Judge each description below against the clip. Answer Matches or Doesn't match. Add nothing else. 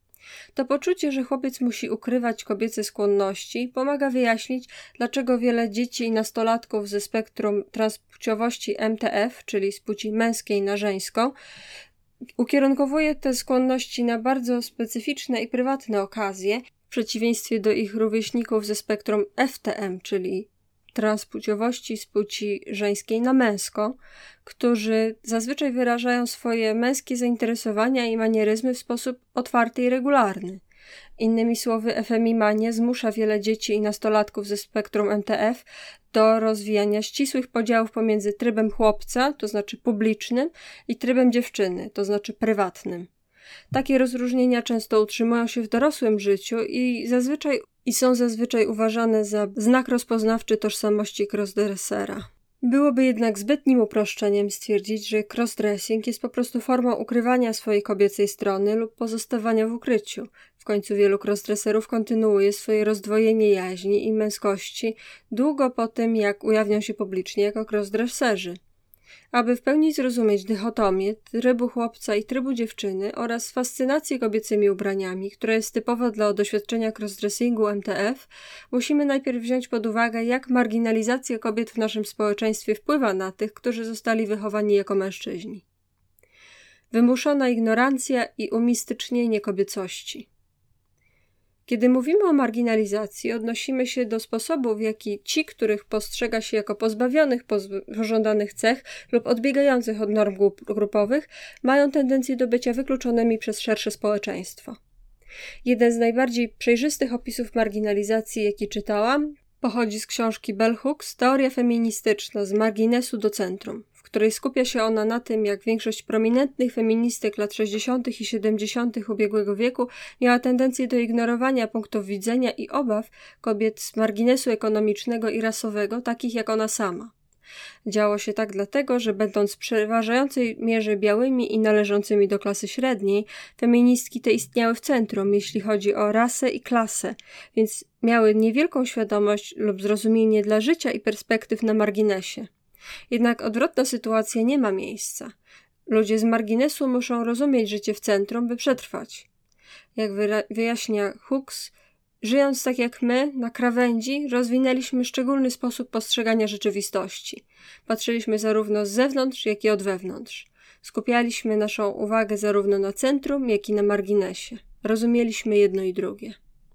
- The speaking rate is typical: Doesn't match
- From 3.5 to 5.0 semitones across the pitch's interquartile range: Doesn't match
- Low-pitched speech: Doesn't match